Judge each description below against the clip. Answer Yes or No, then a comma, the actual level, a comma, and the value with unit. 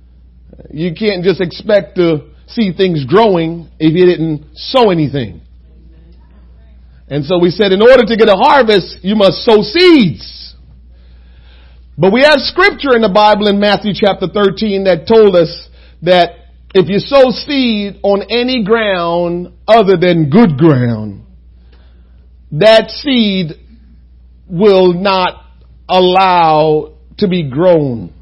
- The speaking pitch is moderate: Yes, medium, 180 Hz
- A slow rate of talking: Yes, slow, 130 wpm